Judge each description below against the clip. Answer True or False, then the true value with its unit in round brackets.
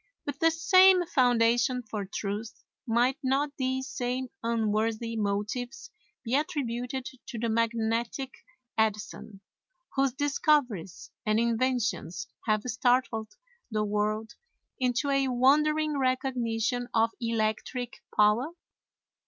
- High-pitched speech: True (240 Hz)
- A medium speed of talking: False (105 wpm)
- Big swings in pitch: False (3.2 semitones)